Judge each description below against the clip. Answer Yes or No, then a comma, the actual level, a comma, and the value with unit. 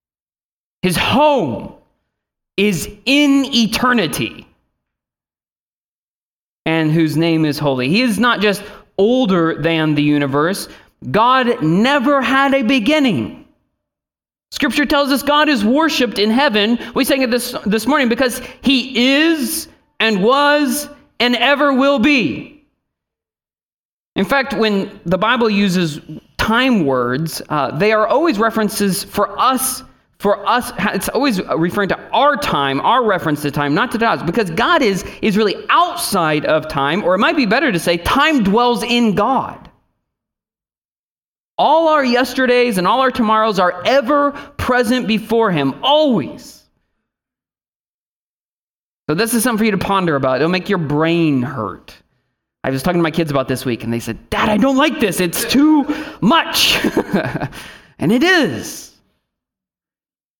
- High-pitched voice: Yes, high, 225 Hz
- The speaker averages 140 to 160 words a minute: Yes, average, 145 wpm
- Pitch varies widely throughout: Yes, wide, 7.1 semitones